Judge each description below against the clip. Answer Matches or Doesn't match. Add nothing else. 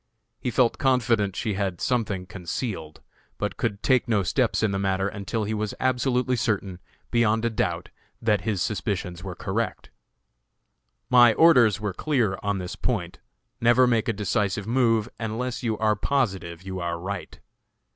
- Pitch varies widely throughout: Doesn't match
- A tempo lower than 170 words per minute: Matches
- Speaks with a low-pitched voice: Matches